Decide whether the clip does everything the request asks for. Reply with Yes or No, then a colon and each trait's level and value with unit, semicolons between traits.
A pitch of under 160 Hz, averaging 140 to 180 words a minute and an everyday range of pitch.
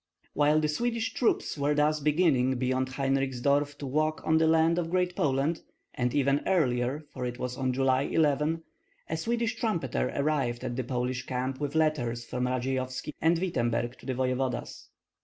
Yes: medium, 140 Hz; average, 170 wpm; average, 3.7 semitones